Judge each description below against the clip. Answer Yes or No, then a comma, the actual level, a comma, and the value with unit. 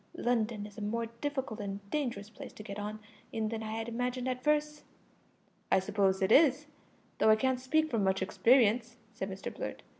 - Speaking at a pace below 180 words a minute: No, average, 190 wpm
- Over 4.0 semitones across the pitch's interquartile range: No, average, 3.6 semitones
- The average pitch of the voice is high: Yes, high, 225 Hz